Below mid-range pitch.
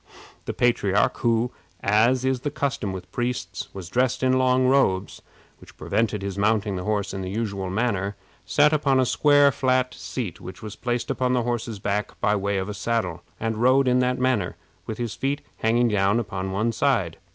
Yes: low, 115 Hz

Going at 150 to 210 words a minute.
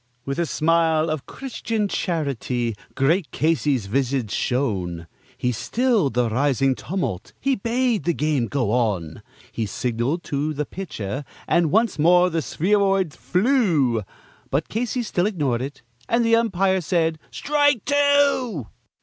No: slow, 135 wpm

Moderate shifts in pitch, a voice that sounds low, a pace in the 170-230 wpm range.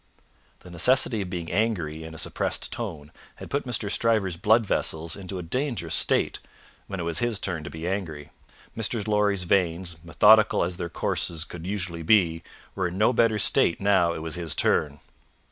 Yes: average, 4.2 semitones; very low, 90 Hz; average, 180 wpm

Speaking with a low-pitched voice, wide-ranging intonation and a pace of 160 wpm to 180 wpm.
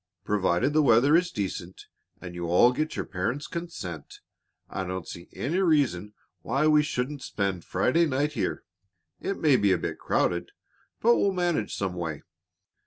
Yes: low, 125 Hz; wide, 8.9 semitones; average, 165 wpm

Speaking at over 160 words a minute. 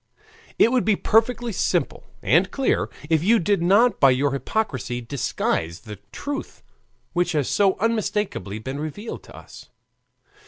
No: average, 145 wpm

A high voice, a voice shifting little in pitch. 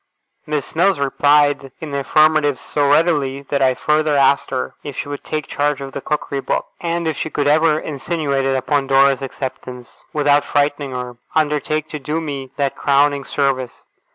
No: medium, 145 Hz; narrow, 1.9 semitones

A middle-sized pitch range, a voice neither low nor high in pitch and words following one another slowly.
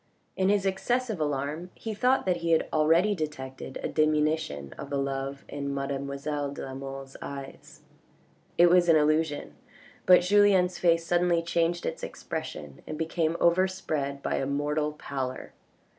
No: average, 3.9 semitones; medium, 155 Hz; average, 145 wpm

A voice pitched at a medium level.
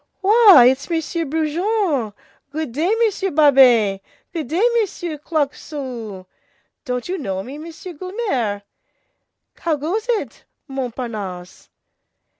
No: very high, 295 Hz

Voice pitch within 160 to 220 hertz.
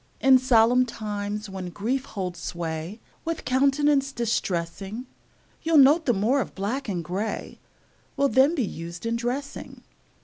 No: high, 230 Hz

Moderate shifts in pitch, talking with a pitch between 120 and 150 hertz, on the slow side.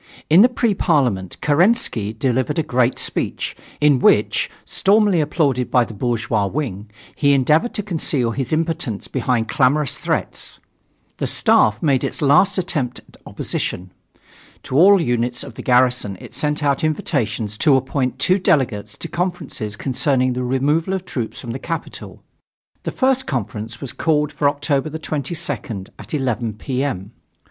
No: average, 4.6 semitones; low, 135 Hz; average, 155 wpm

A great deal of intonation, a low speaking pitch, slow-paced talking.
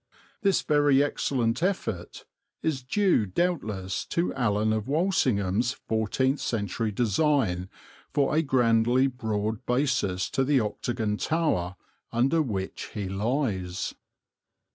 Yes: wide, 5.7 semitones; low, 120 Hz; slow, 110 wpm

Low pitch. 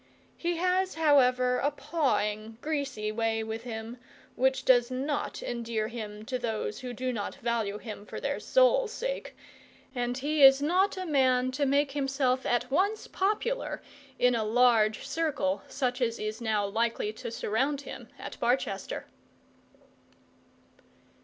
No: very high, 250 Hz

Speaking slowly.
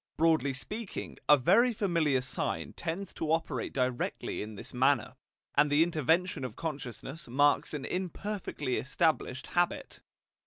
Yes: slow, 130 wpm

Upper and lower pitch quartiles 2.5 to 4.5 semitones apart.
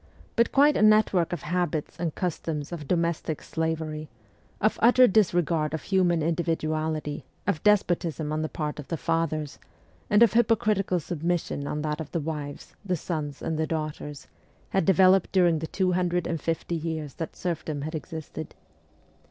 Yes: average, 2.8 semitones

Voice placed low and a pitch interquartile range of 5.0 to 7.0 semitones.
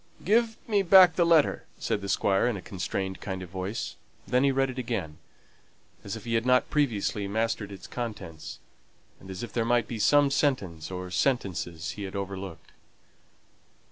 Yes: low, 110 Hz; average, 5.3 semitones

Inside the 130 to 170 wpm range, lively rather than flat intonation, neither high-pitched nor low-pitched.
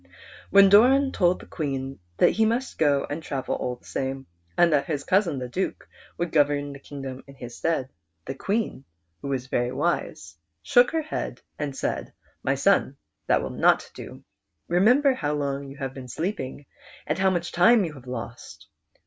No: average, 185 wpm; wide, 5.9 semitones; medium, 145 Hz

